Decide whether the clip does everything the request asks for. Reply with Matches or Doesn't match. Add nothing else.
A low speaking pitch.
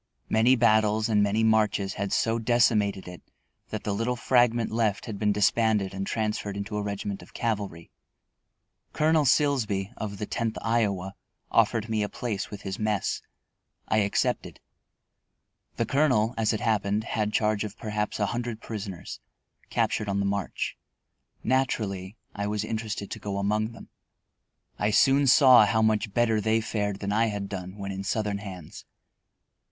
Matches